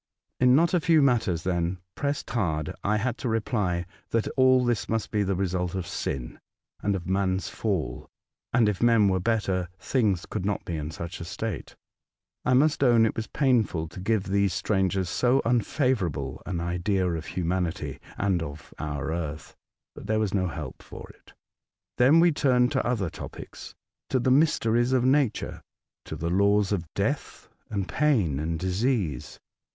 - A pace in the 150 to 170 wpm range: No, average, 180 wpm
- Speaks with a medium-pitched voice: No, low, 100 Hz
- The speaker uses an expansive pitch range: Yes, wide, 5.7 semitones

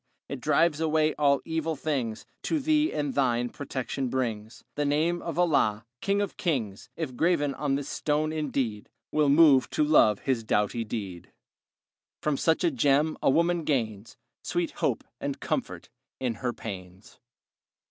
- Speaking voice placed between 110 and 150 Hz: Yes, medium, 140 Hz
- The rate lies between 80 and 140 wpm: No, average, 155 wpm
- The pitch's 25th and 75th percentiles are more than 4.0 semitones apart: Yes, average, 5.1 semitones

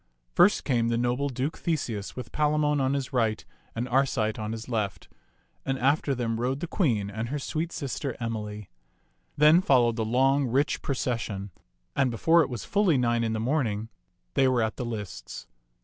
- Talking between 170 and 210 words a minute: Yes, average, 180 wpm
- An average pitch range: Yes, average, 3.8 semitones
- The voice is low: Yes, low, 125 Hz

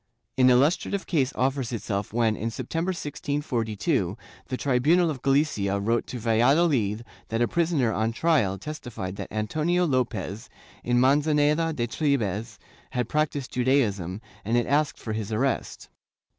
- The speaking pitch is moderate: No, low, 125 Hz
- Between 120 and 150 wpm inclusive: Yes, average, 140 wpm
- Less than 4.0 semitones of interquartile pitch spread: No, average, 5.0 semitones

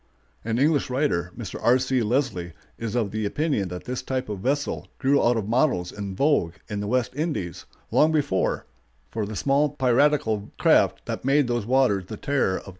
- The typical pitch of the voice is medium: No, low, 120 Hz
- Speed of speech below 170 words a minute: No, average, 190 wpm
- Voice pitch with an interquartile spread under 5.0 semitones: No, wide, 5.4 semitones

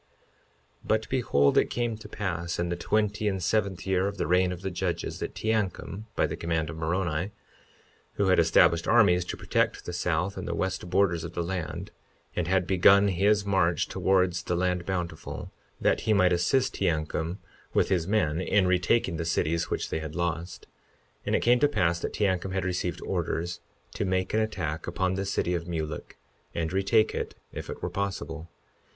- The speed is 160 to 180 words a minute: No, average, 190 wpm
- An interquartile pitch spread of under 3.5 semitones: Yes, average, 2.7 semitones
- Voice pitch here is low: Yes, very low, 90 Hz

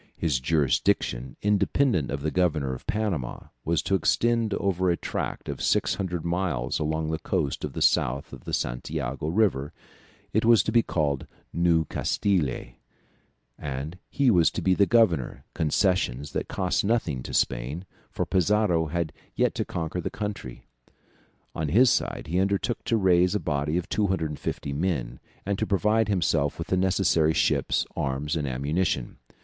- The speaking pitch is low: Yes, very low, 85 Hz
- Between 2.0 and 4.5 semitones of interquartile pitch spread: No, average, 5.1 semitones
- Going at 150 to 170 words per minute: Yes, average, 160 wpm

